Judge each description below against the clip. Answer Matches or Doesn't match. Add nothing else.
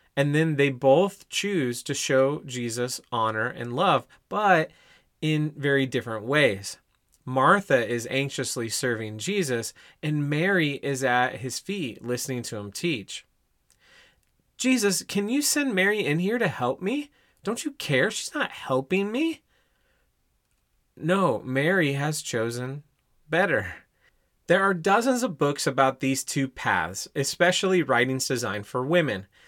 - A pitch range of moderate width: Doesn't match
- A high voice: Doesn't match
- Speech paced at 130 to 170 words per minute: Matches